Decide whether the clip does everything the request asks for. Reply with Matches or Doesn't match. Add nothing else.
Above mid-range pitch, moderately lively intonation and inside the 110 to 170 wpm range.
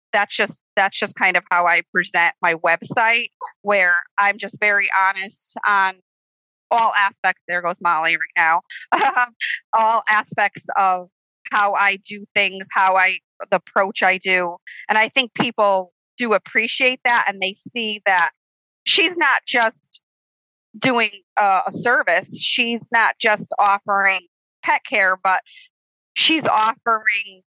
Matches